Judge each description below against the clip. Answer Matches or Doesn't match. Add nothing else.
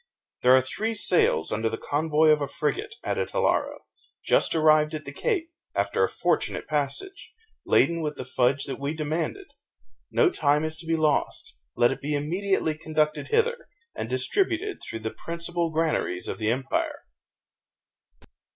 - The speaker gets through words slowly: Doesn't match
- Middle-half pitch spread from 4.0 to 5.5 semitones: Matches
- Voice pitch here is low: Doesn't match